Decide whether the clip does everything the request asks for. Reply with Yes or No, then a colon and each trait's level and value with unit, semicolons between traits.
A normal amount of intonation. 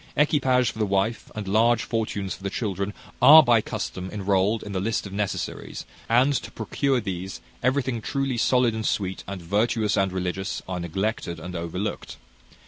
Yes: average, 3.7 semitones